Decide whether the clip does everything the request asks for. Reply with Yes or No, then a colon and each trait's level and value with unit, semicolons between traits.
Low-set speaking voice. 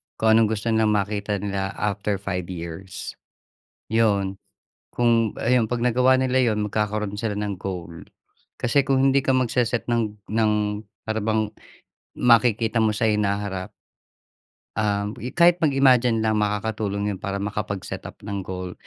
Yes: low, 105 Hz